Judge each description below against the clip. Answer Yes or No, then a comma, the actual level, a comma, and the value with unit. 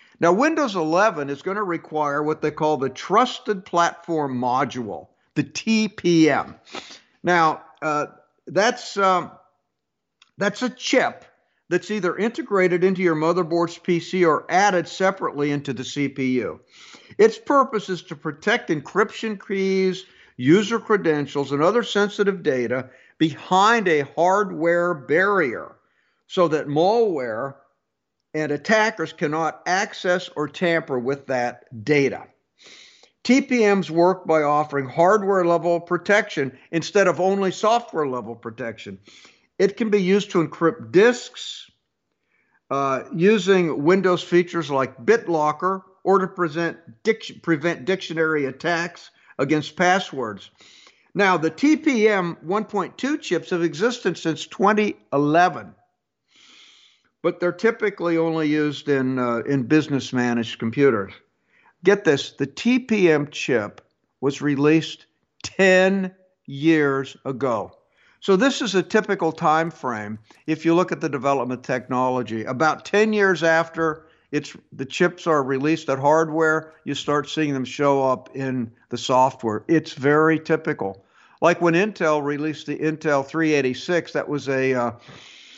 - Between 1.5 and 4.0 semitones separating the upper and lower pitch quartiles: No, average, 4.9 semitones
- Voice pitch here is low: No, medium, 165 Hz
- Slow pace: Yes, slow, 125 wpm